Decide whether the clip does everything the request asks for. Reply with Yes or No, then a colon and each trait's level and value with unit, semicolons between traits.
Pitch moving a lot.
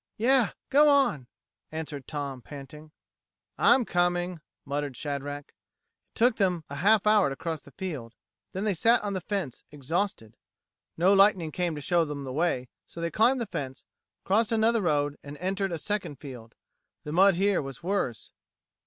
Yes: wide, 5.8 semitones